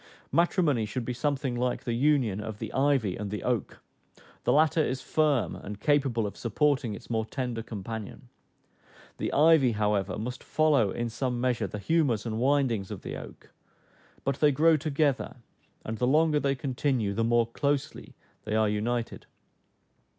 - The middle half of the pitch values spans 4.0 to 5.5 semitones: Yes, average, 4.5 semitones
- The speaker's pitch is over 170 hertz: No, low, 125 Hz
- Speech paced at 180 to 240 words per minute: No, average, 165 wpm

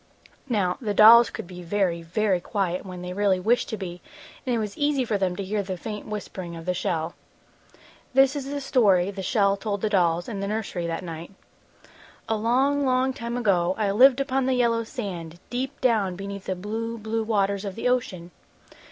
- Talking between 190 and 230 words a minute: Yes, average, 200 wpm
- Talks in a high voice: Yes, high, 205 Hz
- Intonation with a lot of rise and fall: No, average, 4.3 semitones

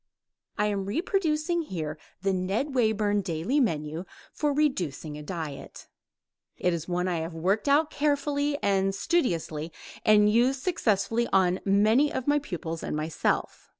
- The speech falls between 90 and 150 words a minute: Yes, average, 145 wpm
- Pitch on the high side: Yes, high, 205 Hz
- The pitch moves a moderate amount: No, wide, 8.7 semitones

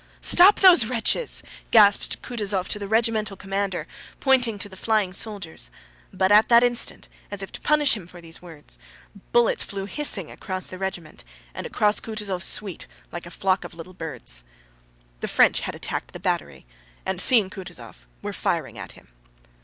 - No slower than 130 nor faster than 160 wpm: No, average, 170 wpm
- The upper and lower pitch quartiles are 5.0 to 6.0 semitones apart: No, average, 3.5 semitones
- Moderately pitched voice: No, high, 200 Hz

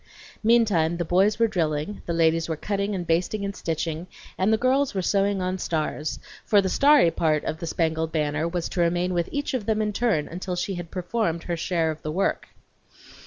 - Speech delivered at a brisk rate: Yes, fast, 210 wpm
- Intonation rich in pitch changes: No, average, 3.8 semitones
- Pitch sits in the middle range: Yes, medium, 175 Hz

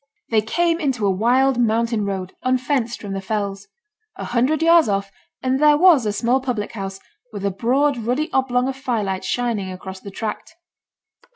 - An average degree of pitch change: Yes, average, 4.8 semitones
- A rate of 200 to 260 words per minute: No, average, 175 wpm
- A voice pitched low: No, high, 235 Hz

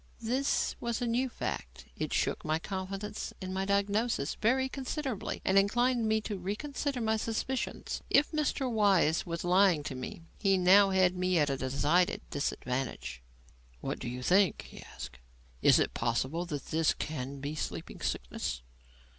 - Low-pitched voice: No, high, 190 Hz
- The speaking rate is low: No, average, 160 wpm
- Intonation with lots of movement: Yes, wide, 6.8 semitones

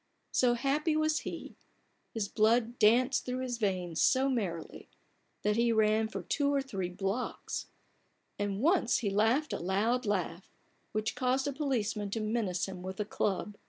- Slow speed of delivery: No, average, 165 wpm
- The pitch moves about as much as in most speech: Yes, average, 4.3 semitones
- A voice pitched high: Yes, high, 220 Hz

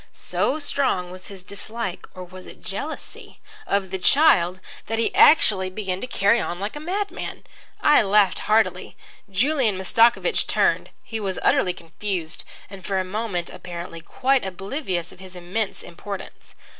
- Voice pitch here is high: Yes, high, 195 Hz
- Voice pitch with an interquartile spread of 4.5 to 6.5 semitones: No, average, 3.9 semitones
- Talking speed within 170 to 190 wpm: No, average, 155 wpm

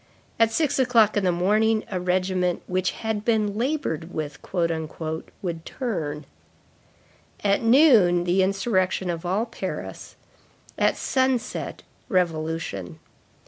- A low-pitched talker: No, medium, 185 Hz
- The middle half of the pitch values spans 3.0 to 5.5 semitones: Yes, average, 4.6 semitones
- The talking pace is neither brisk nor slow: No, slow, 110 wpm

